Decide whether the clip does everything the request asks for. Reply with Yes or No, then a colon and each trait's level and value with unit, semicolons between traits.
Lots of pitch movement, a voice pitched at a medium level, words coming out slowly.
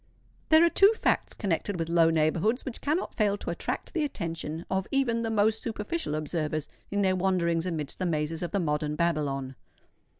No: wide, 5.7 semitones; medium, 175 Hz; average, 180 wpm